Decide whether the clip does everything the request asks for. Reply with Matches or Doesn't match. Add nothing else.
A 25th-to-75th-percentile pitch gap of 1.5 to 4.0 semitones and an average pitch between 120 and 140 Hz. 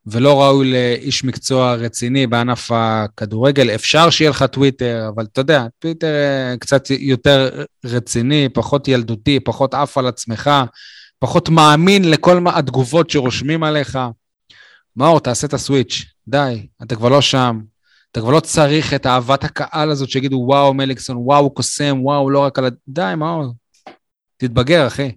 Matches